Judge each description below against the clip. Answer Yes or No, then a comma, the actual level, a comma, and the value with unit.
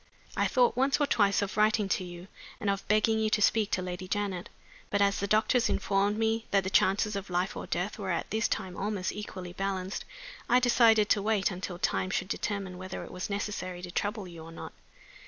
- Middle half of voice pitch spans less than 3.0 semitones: Yes, narrow, 2.6 semitones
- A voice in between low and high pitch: No, high, 200 Hz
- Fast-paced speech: Yes, fast, 215 wpm